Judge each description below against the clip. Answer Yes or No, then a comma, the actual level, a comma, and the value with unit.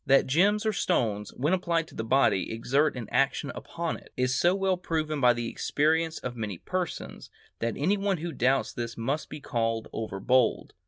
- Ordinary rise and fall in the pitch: No, wide, 6.3 semitones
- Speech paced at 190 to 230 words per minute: Yes, average, 195 wpm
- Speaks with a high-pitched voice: No, medium, 140 Hz